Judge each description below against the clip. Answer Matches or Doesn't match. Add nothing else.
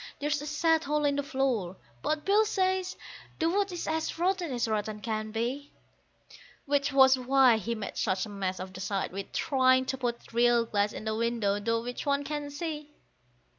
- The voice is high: Matches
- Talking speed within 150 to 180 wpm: Doesn't match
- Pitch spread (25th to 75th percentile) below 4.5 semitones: Doesn't match